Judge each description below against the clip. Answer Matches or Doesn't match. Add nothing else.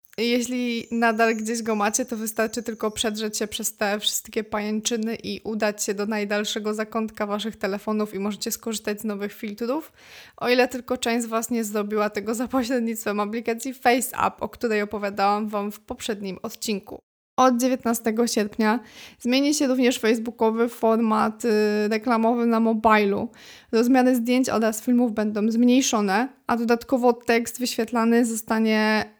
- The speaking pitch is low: Doesn't match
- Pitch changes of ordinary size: Doesn't match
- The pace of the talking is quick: Doesn't match